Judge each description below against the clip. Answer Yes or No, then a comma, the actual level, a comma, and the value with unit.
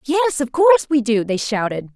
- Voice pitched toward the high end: Yes, very high, 265 Hz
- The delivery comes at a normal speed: No, fast, 215 wpm